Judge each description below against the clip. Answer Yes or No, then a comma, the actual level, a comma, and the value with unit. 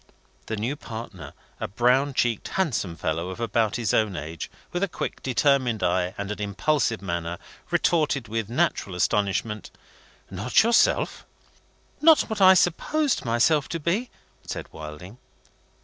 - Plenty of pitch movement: Yes, wide, 7.4 semitones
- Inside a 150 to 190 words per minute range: No, average, 140 wpm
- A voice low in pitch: Yes, low, 115 Hz